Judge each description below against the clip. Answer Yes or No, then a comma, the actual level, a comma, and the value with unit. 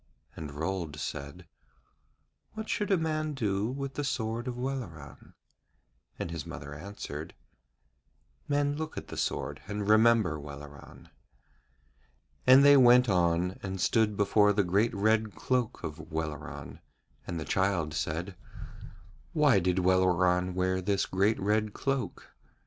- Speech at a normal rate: No, slow, 130 wpm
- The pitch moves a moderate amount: No, wide, 6.0 semitones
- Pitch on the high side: No, low, 100 Hz